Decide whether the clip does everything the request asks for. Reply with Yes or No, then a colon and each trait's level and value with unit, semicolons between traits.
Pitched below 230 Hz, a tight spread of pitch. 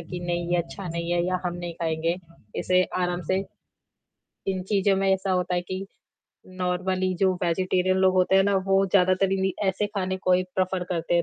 Yes: medium, 185 Hz; narrow, 1.4 semitones